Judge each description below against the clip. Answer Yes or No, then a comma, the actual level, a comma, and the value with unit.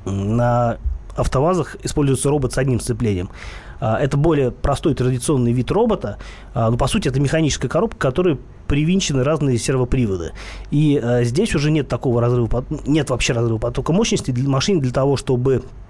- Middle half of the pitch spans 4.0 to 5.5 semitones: No, average, 3.6 semitones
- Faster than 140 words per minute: Yes, average, 150 wpm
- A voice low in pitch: Yes, low, 130 Hz